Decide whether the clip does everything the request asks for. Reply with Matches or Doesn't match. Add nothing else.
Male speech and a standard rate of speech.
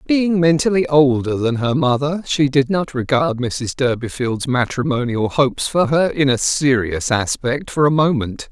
Matches